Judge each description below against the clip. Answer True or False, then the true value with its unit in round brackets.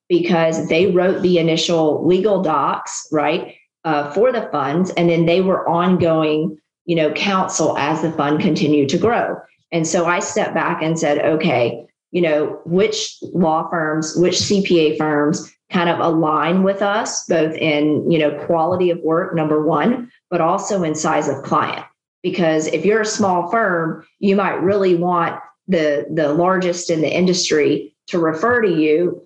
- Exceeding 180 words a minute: False (170 wpm)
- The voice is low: False (170 Hz)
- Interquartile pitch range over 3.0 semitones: False (2.7 semitones)